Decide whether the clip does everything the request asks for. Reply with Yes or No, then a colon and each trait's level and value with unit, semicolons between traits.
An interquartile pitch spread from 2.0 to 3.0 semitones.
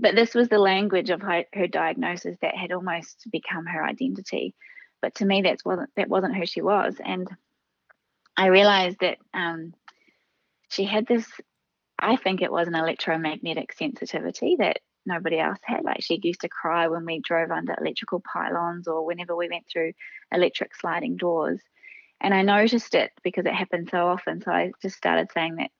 Yes: average, 2.7 semitones